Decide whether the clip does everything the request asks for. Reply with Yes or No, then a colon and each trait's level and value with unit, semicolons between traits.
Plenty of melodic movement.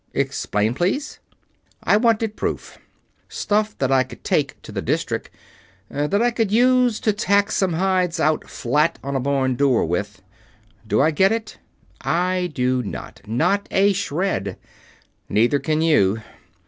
Yes: wide, 7.7 semitones